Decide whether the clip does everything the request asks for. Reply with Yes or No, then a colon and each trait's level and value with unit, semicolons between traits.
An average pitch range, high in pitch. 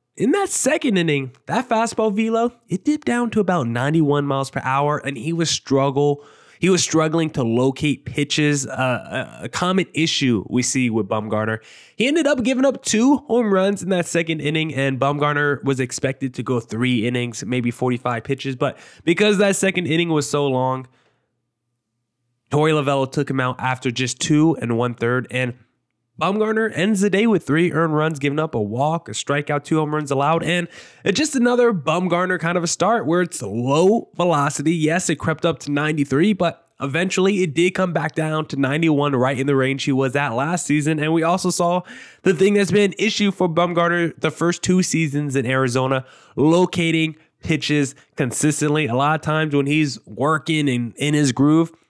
No: average, 4.7 semitones; medium, 155 Hz